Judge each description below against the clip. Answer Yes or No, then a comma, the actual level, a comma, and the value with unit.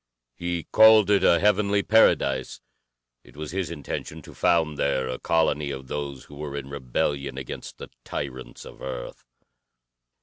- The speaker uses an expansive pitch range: No, average, 4.4 semitones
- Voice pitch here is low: Yes, very low, 75 Hz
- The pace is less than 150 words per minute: No, average, 155 wpm